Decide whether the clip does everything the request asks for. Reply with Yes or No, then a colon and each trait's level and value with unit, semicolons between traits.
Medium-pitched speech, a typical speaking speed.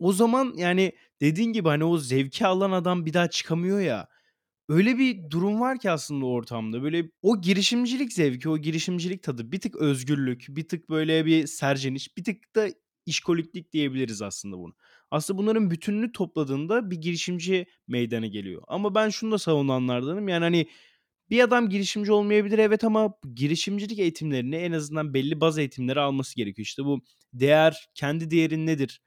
No: medium, 165 Hz; fast, 165 wpm